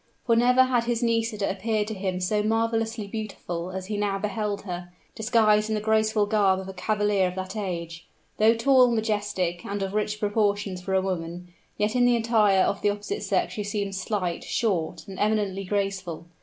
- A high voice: Yes, high, 205 Hz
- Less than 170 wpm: No, average, 190 wpm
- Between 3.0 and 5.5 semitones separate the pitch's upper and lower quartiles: No, narrow, 2.5 semitones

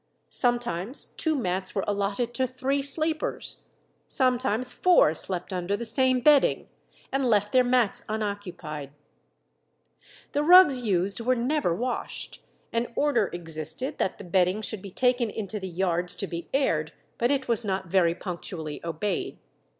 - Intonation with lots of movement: Yes, wide, 5.8 semitones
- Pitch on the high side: Yes, high, 215 Hz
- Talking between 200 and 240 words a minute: No, average, 145 wpm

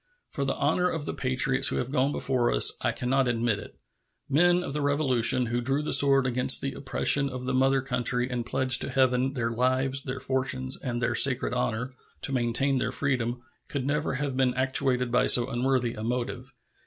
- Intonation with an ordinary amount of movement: No, narrow, 1.7 semitones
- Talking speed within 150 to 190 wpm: No, fast, 205 wpm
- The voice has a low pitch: Yes, low, 130 Hz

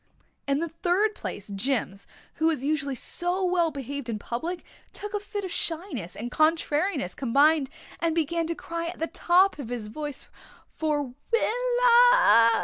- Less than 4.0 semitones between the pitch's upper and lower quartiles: No, average, 4.9 semitones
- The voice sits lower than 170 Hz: No, very high, 320 Hz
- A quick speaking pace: No, average, 155 wpm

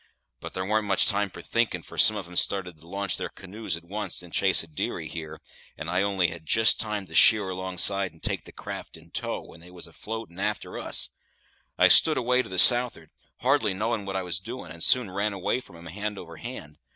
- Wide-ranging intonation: No, average, 3.7 semitones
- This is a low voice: Yes, very low, 95 Hz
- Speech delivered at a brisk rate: Yes, fast, 235 wpm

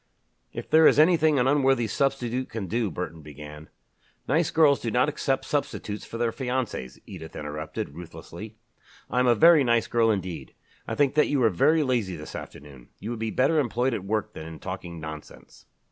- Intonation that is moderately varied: No, wide, 7.8 semitones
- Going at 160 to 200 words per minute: Yes, average, 190 wpm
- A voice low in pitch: Yes, low, 115 Hz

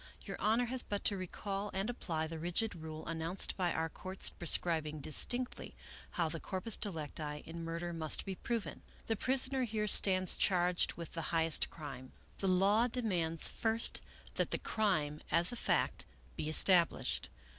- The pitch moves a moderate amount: Yes, average, 4.5 semitones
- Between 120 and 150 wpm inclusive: No, average, 165 wpm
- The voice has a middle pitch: Yes, medium, 180 Hz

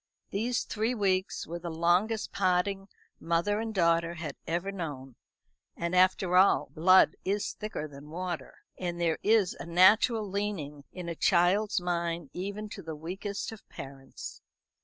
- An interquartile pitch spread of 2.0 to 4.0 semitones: Yes, average, 3.1 semitones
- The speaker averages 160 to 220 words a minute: No, average, 150 wpm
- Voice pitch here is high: No, medium, 180 Hz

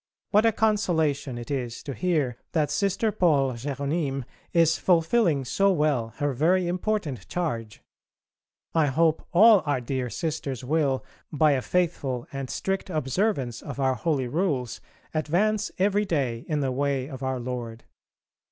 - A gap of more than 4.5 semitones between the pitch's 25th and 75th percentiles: Yes, average, 5.1 semitones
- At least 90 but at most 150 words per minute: Yes, average, 145 wpm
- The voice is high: No, medium, 145 Hz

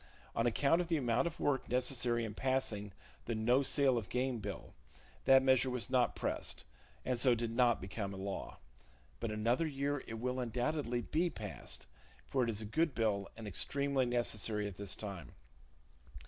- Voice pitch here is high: No, low, 120 Hz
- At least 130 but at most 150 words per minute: No, average, 180 wpm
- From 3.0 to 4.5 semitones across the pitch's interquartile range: Yes, average, 3.5 semitones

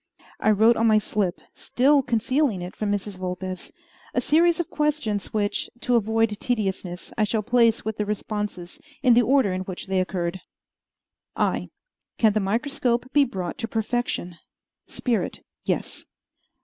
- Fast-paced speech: No, average, 150 wpm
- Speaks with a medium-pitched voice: No, high, 215 Hz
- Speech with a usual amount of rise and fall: Yes, average, 4.1 semitones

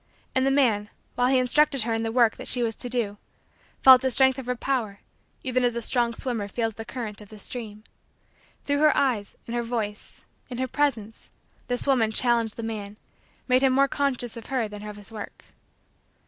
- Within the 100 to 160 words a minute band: No, fast, 205 wpm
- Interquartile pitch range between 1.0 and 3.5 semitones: Yes, average, 2.9 semitones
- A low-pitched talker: No, high, 240 Hz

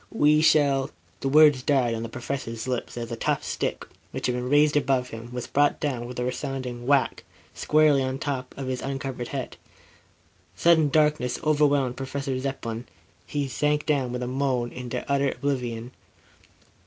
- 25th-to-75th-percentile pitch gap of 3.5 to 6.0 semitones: No, narrow, 2.6 semitones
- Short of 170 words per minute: No, average, 175 wpm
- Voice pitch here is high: No, low, 135 Hz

